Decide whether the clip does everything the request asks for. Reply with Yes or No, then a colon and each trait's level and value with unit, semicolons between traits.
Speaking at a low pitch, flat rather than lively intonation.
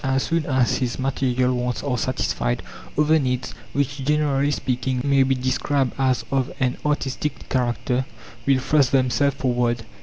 Yes: low, 130 Hz; narrow, 2.0 semitones